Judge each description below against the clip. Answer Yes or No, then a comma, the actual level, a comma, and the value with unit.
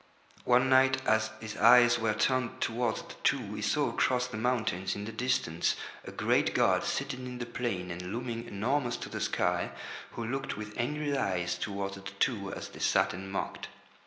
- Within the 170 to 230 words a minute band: Yes, average, 190 wpm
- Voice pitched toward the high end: No, low, 115 Hz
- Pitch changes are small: No, average, 3.9 semitones